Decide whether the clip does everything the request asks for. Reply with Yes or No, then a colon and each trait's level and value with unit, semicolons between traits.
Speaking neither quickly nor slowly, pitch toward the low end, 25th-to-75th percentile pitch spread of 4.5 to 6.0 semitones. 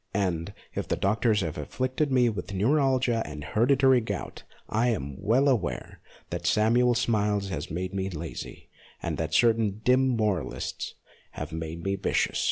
Yes: average, 155 wpm; low, 105 Hz; average, 5.1 semitones